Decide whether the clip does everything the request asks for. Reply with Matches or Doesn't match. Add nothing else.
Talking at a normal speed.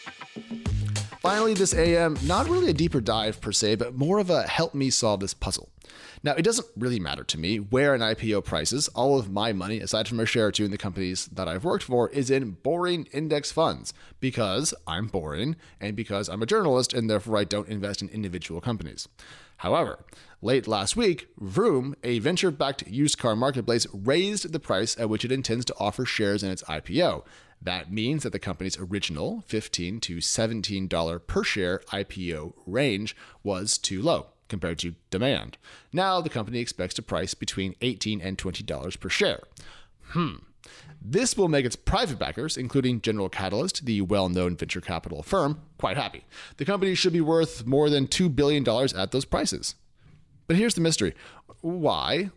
Matches